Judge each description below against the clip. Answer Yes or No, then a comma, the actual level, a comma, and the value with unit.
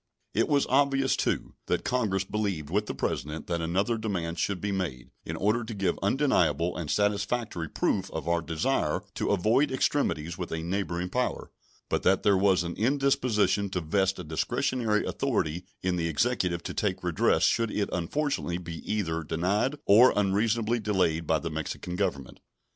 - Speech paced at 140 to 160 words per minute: No, average, 170 wpm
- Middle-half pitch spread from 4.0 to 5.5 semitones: Yes, average, 4.5 semitones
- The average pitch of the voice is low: Yes, very low, 95 Hz